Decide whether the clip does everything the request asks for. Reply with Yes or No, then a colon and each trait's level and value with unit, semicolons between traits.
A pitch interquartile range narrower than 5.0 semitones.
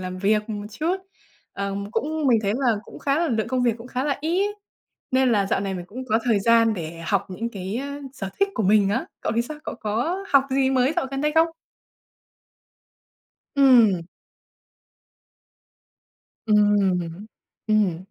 No: average, 5.3 semitones